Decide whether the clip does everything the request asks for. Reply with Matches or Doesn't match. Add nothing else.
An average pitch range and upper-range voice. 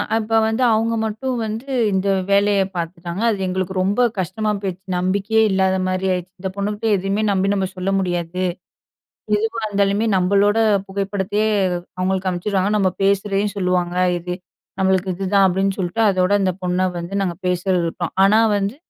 Doesn't match